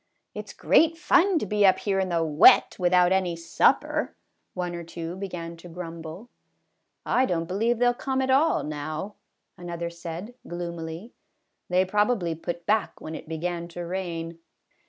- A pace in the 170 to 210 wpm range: Yes, average, 175 wpm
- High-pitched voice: No, medium, 175 Hz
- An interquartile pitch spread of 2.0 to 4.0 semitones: Yes, average, 3.6 semitones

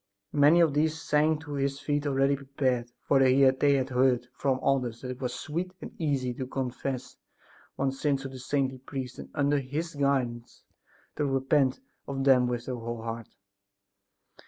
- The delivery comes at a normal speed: Yes, average, 170 wpm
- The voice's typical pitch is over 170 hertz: No, low, 135 Hz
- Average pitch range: No, narrow, 2.1 semitones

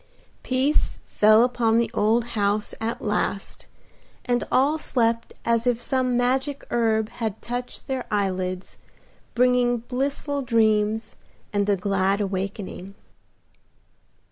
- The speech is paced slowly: Yes, slow, 115 wpm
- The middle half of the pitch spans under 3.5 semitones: Yes, average, 3.1 semitones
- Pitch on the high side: Yes, high, 230 Hz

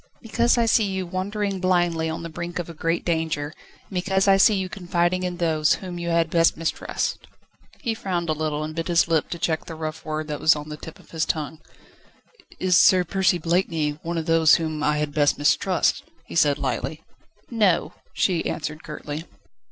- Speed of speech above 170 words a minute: Yes, average, 200 wpm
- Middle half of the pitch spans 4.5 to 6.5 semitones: No, average, 2.9 semitones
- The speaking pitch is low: No, medium, 165 Hz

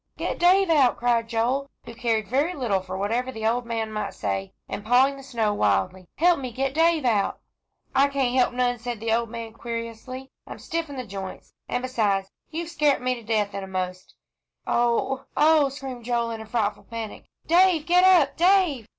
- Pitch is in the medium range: No, high, 245 Hz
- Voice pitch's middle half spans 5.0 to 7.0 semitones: No, average, 4.0 semitones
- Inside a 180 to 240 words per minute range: Yes, average, 190 wpm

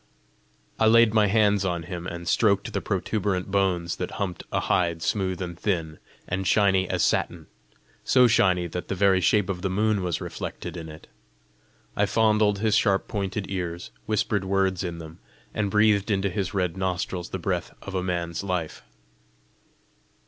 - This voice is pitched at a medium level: No, very low, 95 Hz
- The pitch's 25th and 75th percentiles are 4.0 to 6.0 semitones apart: No, narrow, 2.5 semitones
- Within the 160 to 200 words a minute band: Yes, average, 170 wpm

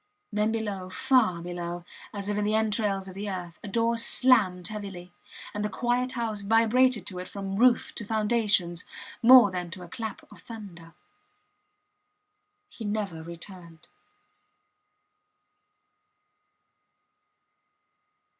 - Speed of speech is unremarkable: No, slow, 125 wpm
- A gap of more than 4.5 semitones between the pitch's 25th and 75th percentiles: No, average, 3.8 semitones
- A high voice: Yes, high, 205 Hz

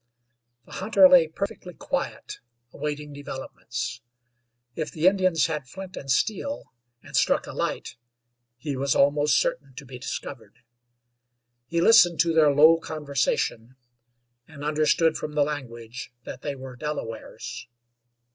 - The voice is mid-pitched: Yes, medium, 150 Hz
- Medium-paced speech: No, slow, 130 wpm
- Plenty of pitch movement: No, average, 3.6 semitones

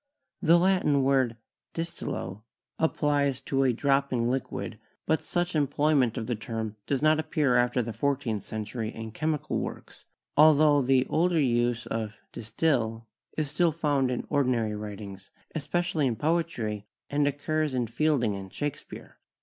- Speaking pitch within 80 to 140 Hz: Yes, low, 135 Hz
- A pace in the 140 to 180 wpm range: Yes, average, 145 wpm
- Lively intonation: No, average, 5.0 semitones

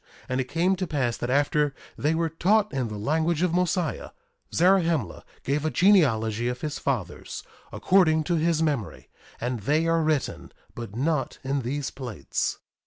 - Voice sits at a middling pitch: Yes, medium, 150 Hz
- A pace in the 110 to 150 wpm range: No, average, 165 wpm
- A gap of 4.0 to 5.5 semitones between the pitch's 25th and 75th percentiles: Yes, average, 4.8 semitones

